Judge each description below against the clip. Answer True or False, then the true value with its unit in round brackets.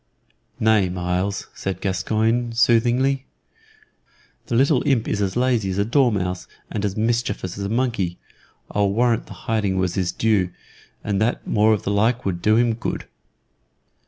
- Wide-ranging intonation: False (3.5 semitones)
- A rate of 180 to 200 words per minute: False (160 wpm)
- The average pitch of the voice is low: True (110 Hz)